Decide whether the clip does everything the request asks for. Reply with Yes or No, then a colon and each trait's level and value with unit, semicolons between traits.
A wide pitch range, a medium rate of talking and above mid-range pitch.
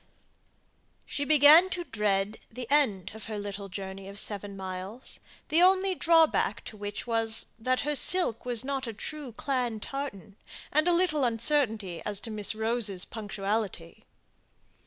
Yes: wide, 6.0 semitones; average, 150 wpm; high, 225 Hz